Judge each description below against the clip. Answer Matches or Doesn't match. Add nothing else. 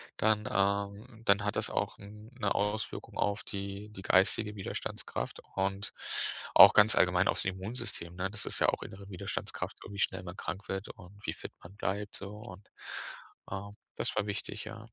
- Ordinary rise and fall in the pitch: Doesn't match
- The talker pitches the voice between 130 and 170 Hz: Doesn't match